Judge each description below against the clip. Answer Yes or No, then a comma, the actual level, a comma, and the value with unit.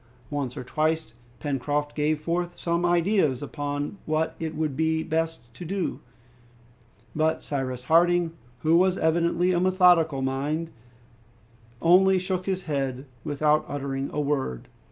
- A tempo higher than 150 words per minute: No, slow, 135 wpm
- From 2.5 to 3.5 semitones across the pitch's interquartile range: Yes, average, 3.2 semitones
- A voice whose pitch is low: No, medium, 160 Hz